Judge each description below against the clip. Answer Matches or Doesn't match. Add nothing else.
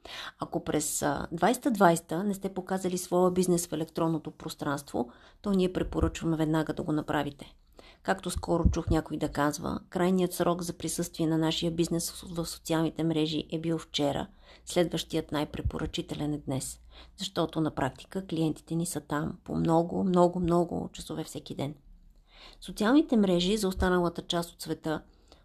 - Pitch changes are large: Doesn't match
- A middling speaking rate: Matches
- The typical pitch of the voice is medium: Matches